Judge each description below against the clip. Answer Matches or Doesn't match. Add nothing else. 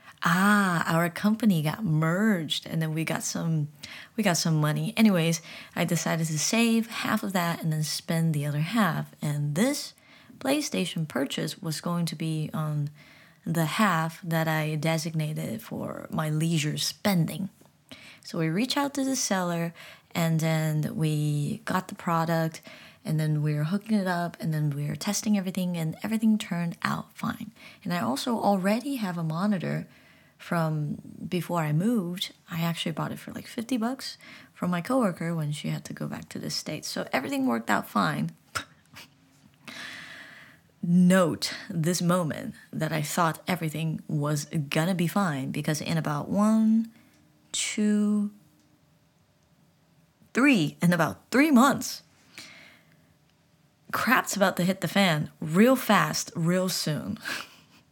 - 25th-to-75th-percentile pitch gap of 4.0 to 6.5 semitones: Matches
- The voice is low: Doesn't match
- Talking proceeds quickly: Doesn't match